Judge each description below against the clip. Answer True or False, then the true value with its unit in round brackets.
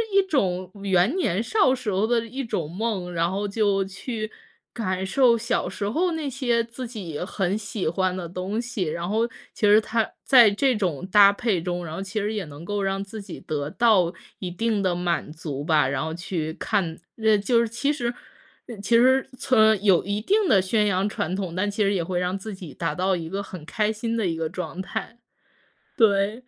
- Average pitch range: True (4.2 semitones)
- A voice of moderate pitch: False (200 Hz)